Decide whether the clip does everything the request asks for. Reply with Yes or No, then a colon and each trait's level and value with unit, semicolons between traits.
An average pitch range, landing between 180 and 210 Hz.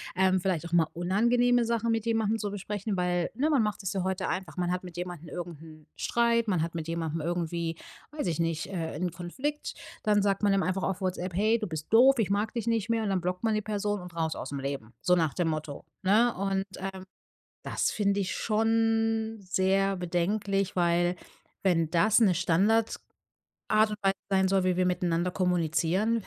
Yes: average, 3.6 semitones; high, 190 Hz